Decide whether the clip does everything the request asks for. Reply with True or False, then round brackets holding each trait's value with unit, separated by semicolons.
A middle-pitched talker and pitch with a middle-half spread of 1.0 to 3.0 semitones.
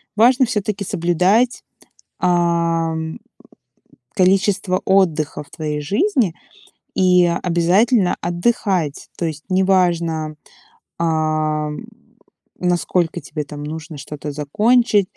False (175 Hz; 3.7 semitones)